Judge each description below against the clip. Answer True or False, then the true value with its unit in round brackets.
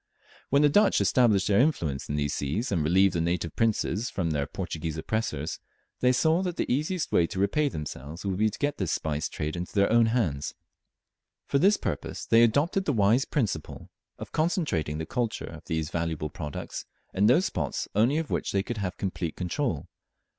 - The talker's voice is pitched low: True (100 Hz)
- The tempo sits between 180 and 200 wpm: True (190 wpm)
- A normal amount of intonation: False (7.9 semitones)